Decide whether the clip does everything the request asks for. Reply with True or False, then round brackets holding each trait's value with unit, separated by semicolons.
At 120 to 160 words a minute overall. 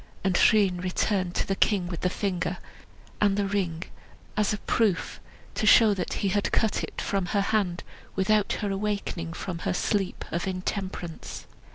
False (175 wpm)